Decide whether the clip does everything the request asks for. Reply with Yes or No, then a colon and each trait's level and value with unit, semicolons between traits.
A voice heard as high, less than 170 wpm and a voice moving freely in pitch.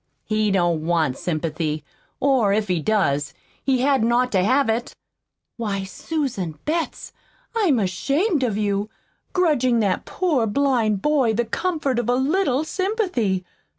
Yes: high, 235 Hz; average, 140 wpm; wide, 6.4 semitones